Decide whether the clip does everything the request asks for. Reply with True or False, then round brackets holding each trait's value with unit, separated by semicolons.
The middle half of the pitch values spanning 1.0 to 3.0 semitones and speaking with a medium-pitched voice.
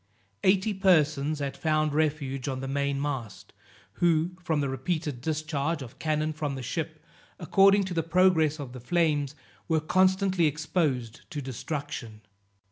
False (3.4 semitones; 155 Hz)